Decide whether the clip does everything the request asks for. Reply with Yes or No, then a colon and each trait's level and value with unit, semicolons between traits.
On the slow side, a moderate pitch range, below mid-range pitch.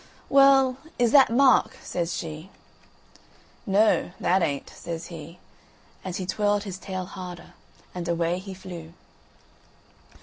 No: slow, 125 wpm; average, 3.4 semitones; medium, 185 Hz